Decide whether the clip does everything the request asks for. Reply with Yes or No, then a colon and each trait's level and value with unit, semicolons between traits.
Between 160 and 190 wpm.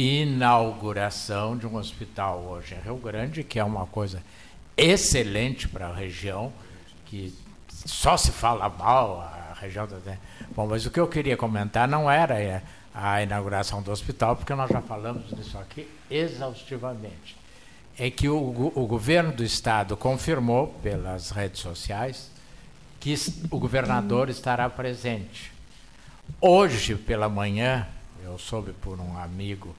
No: average, 135 wpm